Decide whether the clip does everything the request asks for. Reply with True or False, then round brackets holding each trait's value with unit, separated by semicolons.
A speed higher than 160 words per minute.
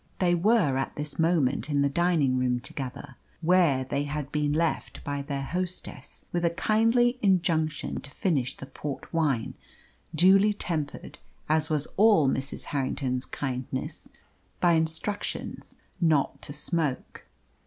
False (135 wpm)